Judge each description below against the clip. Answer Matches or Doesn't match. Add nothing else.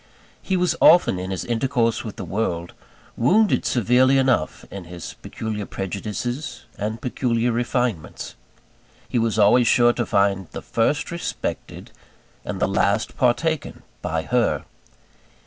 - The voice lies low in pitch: Matches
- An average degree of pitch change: Matches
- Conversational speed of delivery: Doesn't match